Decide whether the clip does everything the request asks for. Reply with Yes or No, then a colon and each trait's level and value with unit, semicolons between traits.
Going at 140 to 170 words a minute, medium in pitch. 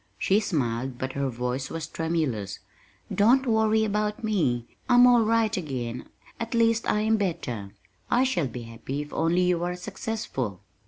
Yes: average, 160 wpm; medium, 170 Hz